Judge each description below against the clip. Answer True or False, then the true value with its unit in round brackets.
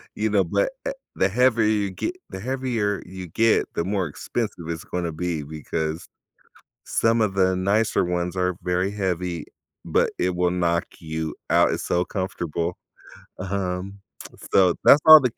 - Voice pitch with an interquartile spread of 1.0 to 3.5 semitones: True (3.0 semitones)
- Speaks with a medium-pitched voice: False (90 Hz)